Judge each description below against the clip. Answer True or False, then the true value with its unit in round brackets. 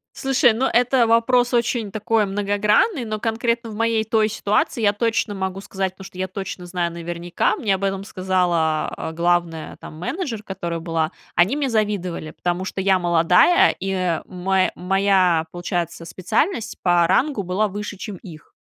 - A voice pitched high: True (195 Hz)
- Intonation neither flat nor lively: True (4.1 semitones)